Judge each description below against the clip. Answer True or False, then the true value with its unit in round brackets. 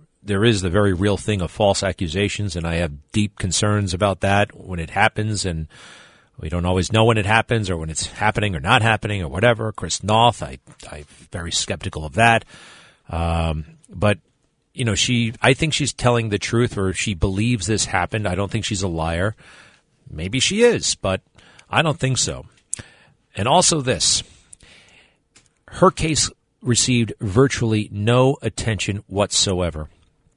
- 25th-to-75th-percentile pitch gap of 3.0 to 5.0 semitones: True (4.2 semitones)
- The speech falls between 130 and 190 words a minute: True (165 wpm)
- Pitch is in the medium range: False (105 Hz)